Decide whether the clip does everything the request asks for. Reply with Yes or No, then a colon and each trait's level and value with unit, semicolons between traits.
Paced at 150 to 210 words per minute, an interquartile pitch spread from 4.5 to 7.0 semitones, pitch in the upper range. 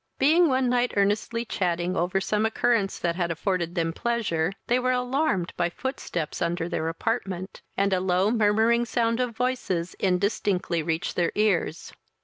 Yes: average, 155 wpm; average, 5.3 semitones; high, 200 Hz